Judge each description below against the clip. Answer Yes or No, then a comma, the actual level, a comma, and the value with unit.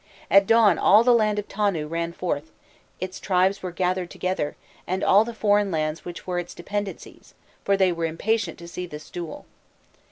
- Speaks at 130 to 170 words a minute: No, average, 185 wpm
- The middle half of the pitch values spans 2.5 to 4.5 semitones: Yes, average, 3.2 semitones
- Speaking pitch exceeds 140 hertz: Yes, medium, 185 Hz